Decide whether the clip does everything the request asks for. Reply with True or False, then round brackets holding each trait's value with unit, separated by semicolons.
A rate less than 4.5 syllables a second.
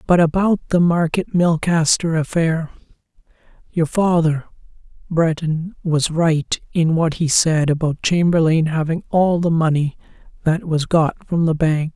True (4.2 syllables/s)